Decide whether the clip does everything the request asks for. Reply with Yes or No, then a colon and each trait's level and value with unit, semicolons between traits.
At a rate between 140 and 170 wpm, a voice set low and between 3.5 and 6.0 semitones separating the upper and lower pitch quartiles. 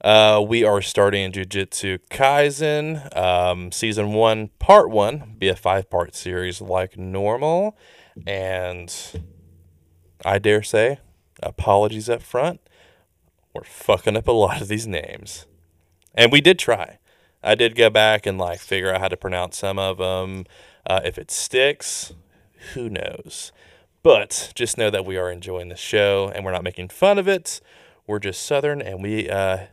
No: average, 160 wpm; very low, 95 Hz; average, 3.1 semitones